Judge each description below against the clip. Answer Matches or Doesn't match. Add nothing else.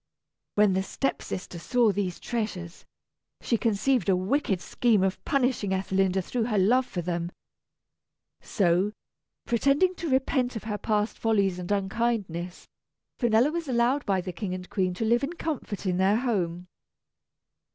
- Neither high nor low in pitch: Doesn't match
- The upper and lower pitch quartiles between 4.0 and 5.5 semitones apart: Matches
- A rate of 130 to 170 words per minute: Matches